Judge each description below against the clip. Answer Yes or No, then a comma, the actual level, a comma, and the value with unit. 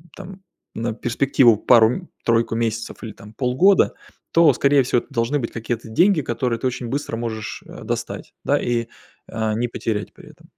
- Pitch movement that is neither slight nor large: Yes, average, 3.2 semitones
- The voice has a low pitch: Yes, low, 120 Hz